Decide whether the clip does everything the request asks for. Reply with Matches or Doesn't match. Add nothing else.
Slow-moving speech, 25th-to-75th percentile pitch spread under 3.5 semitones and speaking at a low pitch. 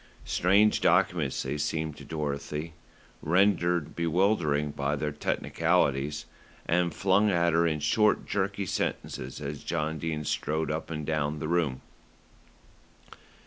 Matches